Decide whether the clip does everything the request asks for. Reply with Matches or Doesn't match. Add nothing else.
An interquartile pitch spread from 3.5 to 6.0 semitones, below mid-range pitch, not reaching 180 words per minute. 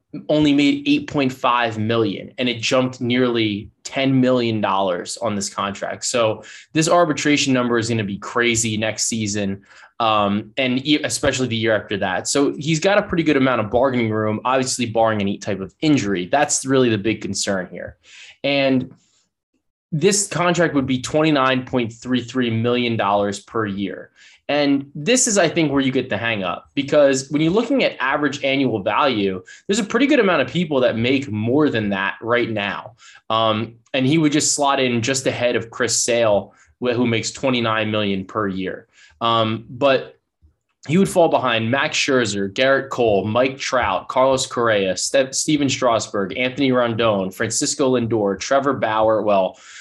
Matches